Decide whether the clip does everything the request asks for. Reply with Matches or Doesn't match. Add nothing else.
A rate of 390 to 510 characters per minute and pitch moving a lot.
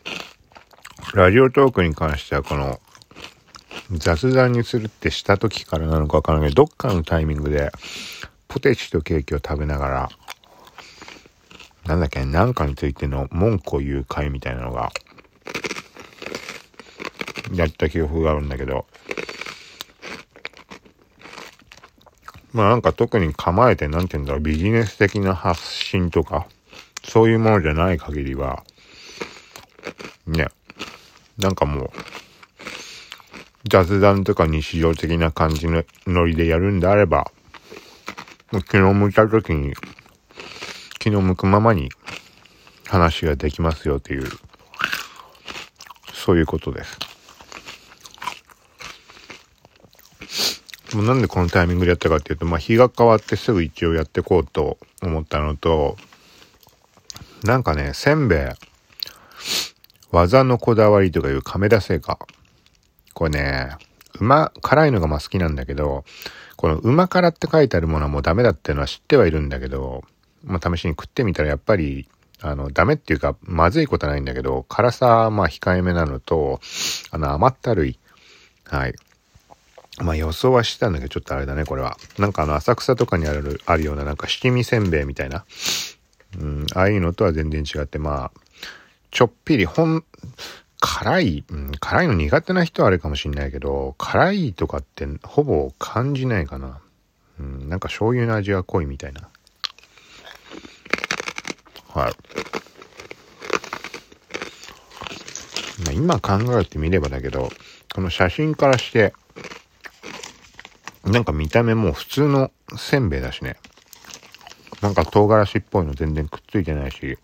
Doesn't match